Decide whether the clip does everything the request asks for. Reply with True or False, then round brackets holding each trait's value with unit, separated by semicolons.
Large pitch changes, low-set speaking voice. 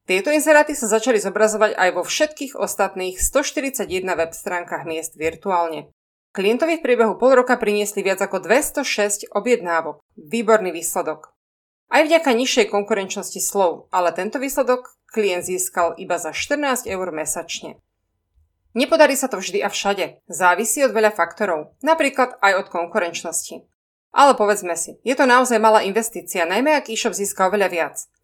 False (5.8 semitones; 200 Hz)